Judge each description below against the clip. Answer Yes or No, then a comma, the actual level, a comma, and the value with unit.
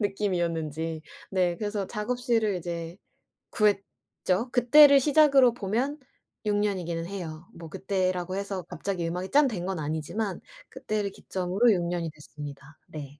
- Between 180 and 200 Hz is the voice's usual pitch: Yes, high, 190 Hz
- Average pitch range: Yes, average, 4.2 semitones